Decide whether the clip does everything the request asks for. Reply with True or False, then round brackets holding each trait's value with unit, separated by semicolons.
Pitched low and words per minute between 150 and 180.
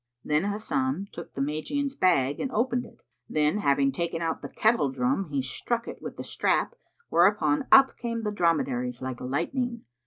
False (170 Hz; 175 wpm)